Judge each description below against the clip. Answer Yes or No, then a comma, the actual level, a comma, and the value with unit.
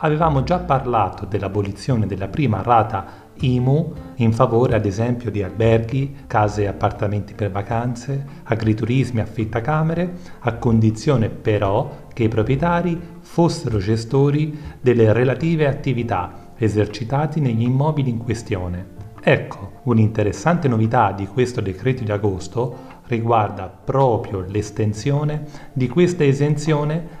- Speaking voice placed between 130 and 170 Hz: No, low, 115 Hz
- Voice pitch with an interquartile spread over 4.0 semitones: Yes, average, 4.9 semitones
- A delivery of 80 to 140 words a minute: Yes, slow, 115 wpm